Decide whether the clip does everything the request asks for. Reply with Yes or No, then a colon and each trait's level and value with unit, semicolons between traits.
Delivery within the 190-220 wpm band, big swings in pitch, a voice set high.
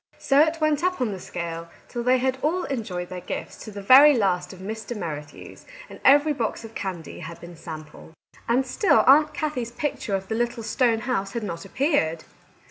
Yes: average, 200 wpm; wide, 7.2 semitones; high, 225 Hz